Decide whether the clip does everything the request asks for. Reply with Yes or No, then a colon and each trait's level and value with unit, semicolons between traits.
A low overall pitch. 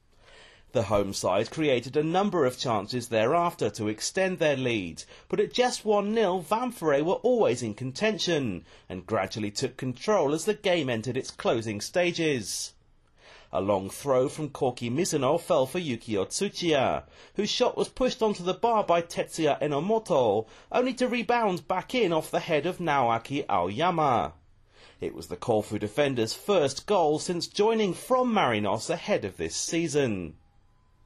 No: medium, 155 Hz